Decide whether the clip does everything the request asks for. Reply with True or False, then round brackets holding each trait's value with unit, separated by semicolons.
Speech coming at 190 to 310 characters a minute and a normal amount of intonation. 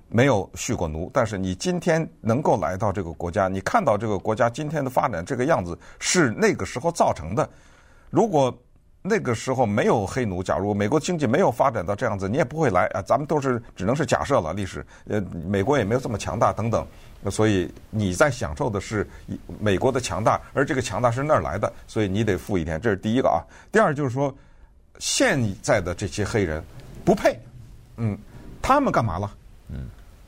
True (305 characters per minute; 4.8 semitones)